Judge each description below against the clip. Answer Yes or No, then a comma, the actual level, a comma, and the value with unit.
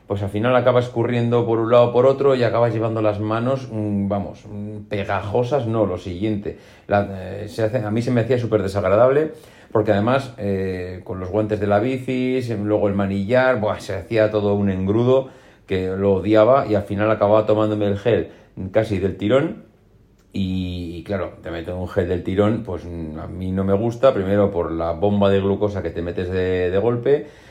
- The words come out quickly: Yes, fast, 195 wpm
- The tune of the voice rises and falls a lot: No, average, 3.0 semitones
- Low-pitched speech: Yes, low, 105 Hz